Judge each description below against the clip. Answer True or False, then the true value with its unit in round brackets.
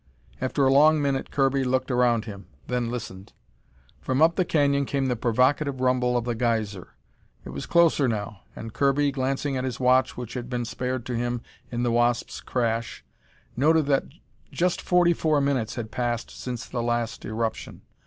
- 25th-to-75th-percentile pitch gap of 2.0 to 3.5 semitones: True (2.8 semitones)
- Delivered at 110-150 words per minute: False (175 wpm)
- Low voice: True (125 Hz)